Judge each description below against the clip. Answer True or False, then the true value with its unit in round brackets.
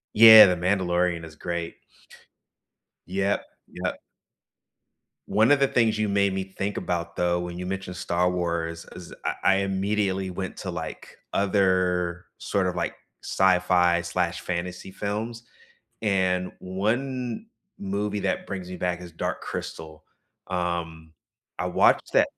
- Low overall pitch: True (90 Hz)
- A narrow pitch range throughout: True (2.3 semitones)